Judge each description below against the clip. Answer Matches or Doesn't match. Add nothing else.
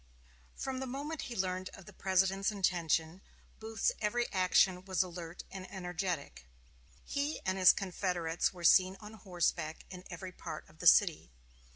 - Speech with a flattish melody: Matches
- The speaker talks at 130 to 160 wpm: Matches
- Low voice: Doesn't match